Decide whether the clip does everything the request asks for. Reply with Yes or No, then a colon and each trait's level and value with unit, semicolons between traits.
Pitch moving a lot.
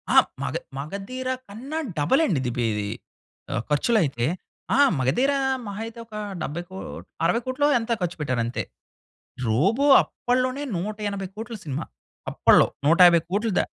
Yes: wide, 8.1 semitones